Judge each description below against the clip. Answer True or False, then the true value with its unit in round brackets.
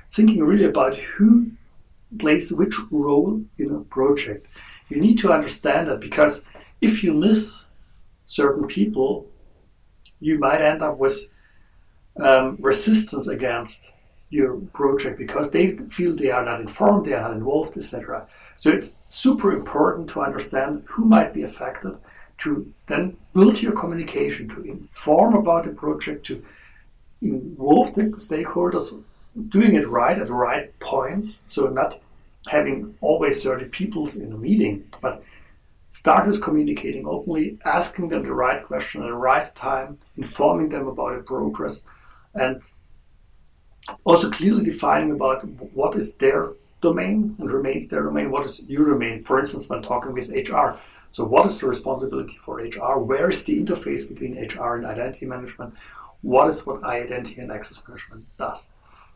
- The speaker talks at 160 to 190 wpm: False (150 wpm)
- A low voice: False (145 Hz)